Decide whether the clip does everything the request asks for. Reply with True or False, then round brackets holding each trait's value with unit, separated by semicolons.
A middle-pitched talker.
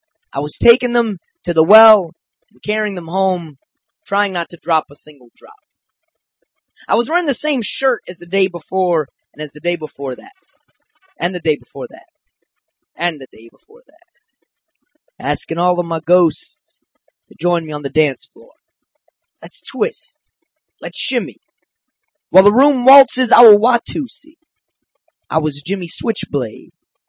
False (195 Hz)